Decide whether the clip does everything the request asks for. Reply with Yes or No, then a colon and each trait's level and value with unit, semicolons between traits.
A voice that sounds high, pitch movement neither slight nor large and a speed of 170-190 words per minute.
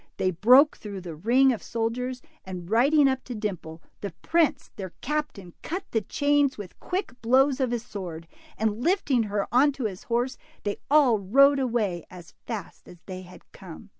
No: high, 230 Hz; wide, 5.9 semitones; average, 180 wpm